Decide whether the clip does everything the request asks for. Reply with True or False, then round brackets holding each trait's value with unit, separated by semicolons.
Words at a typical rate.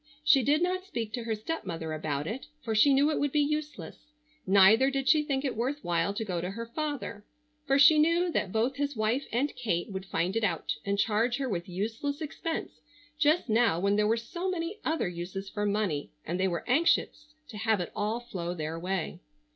False (210 wpm)